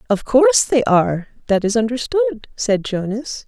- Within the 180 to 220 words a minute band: No, average, 155 wpm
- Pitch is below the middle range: No, high, 240 Hz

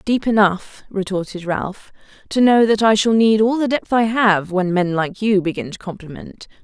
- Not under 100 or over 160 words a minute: No, average, 200 wpm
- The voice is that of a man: No, female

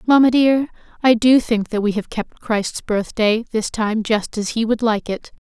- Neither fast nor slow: No, fast, 210 wpm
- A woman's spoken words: Yes, female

